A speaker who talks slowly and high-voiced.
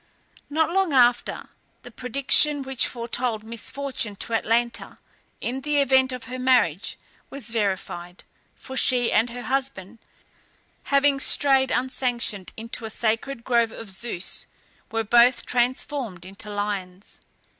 Yes: slow, 125 wpm; high, 240 Hz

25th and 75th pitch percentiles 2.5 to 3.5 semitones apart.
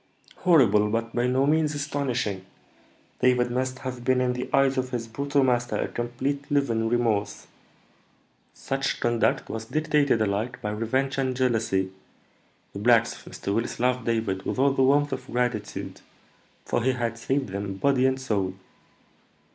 Yes: average, 3.0 semitones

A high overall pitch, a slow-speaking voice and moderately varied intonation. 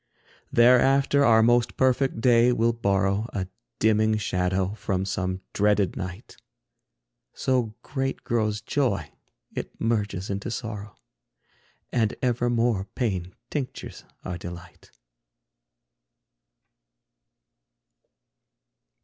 No: low, 110 Hz; slow, 90 wpm; average, 3.8 semitones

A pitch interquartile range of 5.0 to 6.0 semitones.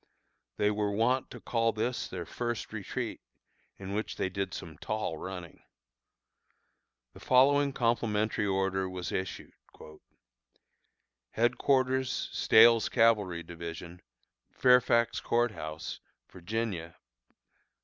No: average, 4.3 semitones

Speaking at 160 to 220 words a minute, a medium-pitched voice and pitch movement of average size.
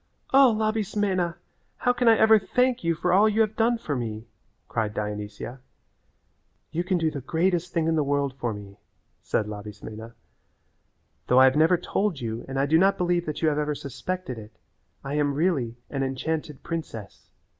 No: average, 180 wpm; medium, 155 Hz; wide, 6.8 semitones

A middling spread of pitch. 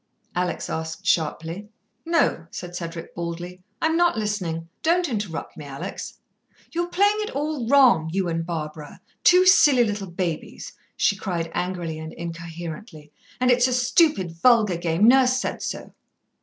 No: wide, 7.4 semitones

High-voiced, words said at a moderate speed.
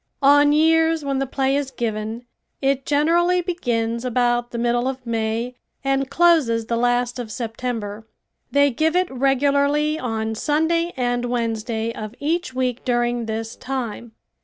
Yes: very high, 250 Hz; average, 145 wpm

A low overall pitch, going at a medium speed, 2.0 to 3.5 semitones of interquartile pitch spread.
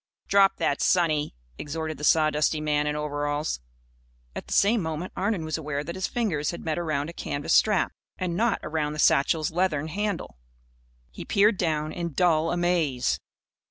No: medium, 160 Hz; average, 165 wpm; average, 3.1 semitones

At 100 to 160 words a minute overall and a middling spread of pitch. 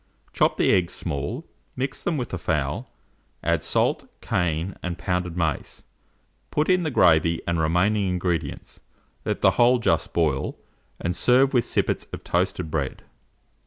No: average, 150 wpm; wide, 6.5 semitones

